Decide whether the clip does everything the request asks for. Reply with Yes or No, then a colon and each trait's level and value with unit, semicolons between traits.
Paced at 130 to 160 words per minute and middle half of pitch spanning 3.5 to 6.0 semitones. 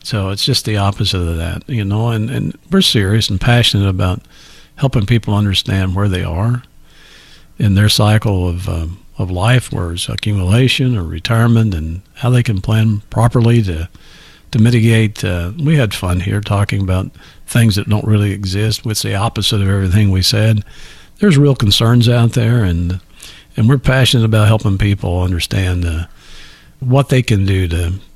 No: average, 175 wpm; average, 3.8 semitones